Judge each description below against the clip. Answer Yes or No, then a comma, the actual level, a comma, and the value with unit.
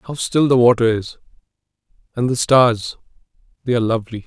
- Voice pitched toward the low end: Yes, low, 120 Hz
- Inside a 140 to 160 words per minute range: Yes, average, 155 wpm